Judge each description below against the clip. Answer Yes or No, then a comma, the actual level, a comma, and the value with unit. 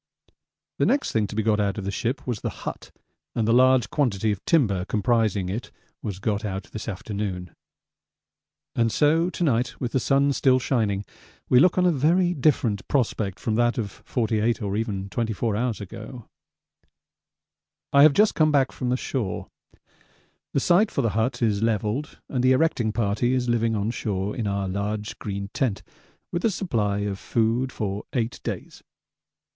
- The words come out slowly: No, average, 175 wpm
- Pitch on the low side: Yes, low, 115 Hz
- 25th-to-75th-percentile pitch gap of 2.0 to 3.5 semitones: No, average, 4.1 semitones